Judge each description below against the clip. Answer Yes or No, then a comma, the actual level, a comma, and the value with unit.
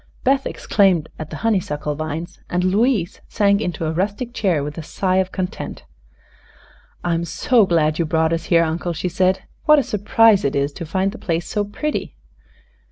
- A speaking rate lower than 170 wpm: No, average, 180 wpm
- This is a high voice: No, medium, 180 Hz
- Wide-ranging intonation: No, average, 4.0 semitones